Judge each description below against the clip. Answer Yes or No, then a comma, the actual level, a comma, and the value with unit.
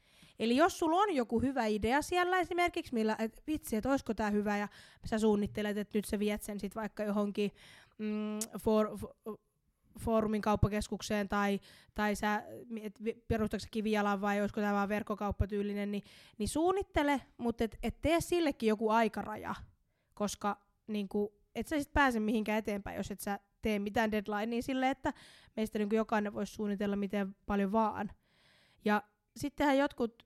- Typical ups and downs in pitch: No, narrow, 2.2 semitones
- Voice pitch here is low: No, high, 215 Hz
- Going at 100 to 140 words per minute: No, fast, 155 wpm